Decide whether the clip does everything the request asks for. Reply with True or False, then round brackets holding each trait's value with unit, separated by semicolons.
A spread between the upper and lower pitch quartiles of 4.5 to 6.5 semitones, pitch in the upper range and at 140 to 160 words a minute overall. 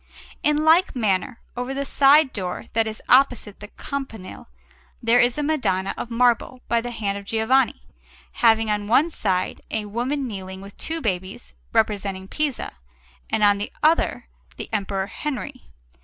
True (5.0 semitones; 230 Hz; 155 wpm)